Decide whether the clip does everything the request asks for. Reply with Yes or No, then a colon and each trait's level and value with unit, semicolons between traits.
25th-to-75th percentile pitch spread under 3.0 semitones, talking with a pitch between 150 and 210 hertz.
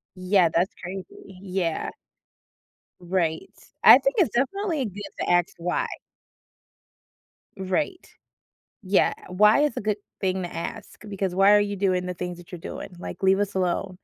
Yes: narrow, 2.4 semitones; high, 190 Hz